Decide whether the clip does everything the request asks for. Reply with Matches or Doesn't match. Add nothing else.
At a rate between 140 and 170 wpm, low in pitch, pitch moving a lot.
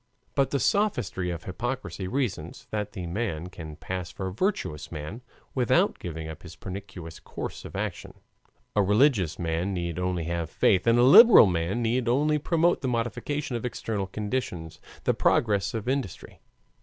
Matches